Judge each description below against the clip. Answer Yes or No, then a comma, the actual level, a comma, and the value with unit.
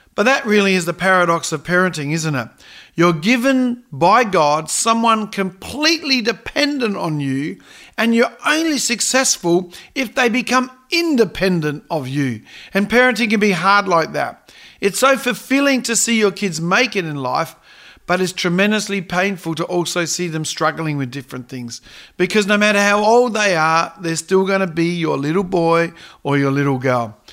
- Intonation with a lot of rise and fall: Yes, wide, 6.1 semitones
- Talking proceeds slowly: No, average, 170 wpm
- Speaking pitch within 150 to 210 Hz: Yes, high, 190 Hz